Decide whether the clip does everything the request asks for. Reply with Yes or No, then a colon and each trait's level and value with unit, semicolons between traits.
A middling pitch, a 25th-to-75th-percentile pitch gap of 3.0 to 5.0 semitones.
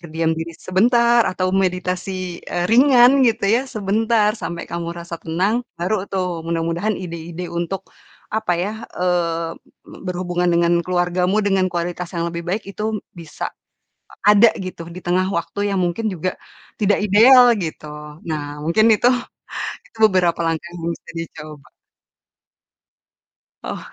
Yes: medium, 180 Hz; average, 3.4 semitones